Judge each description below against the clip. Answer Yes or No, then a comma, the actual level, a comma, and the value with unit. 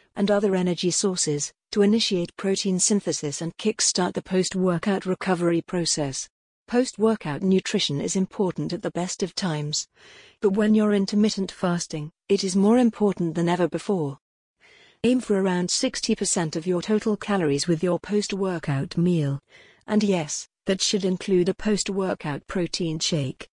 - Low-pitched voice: No, medium, 185 Hz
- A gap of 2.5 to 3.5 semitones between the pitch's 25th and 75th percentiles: Yes, average, 3.2 semitones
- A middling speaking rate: Yes, average, 155 wpm